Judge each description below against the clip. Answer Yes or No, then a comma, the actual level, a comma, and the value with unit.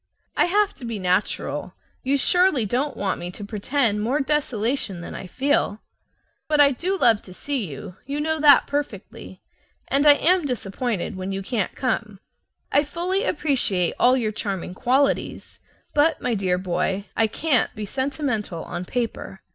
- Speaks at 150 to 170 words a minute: Yes, average, 165 wpm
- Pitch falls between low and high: No, high, 245 Hz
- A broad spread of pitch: Yes, wide, 6.5 semitones